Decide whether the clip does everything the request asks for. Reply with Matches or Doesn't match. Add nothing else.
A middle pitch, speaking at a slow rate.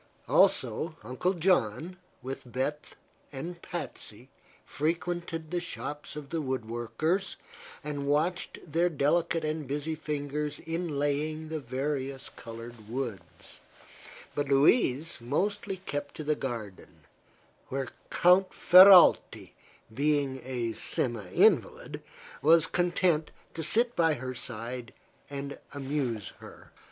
Matches